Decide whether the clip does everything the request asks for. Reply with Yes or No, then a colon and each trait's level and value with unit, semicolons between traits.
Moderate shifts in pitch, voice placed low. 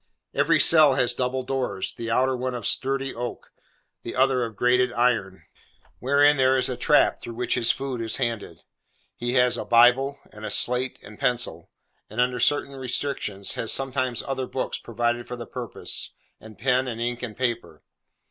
No: narrow, 2.0 semitones; low, 125 Hz